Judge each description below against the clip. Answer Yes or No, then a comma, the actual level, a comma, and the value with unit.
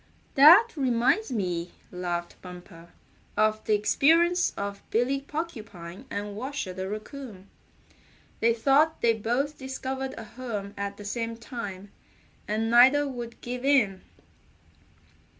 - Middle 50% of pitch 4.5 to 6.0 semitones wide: Yes, average, 5.0 semitones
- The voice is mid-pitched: No, high, 230 Hz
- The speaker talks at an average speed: No, slow, 120 wpm